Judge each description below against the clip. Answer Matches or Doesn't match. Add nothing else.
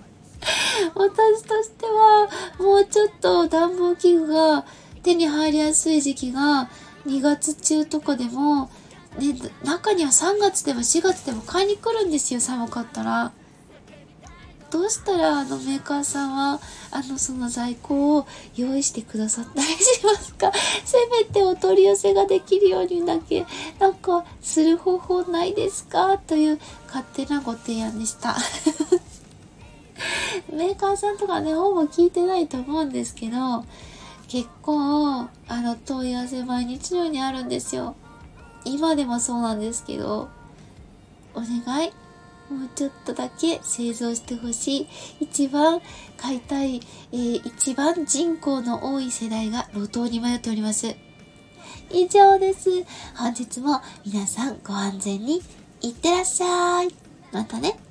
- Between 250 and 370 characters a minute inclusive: Matches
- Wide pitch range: Matches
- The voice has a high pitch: Matches